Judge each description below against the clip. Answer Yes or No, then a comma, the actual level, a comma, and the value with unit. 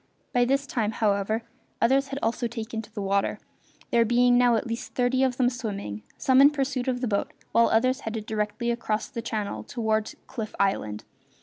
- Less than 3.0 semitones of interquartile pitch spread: Yes, narrow, 2.6 semitones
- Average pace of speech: Yes, average, 190 wpm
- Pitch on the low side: No, high, 230 Hz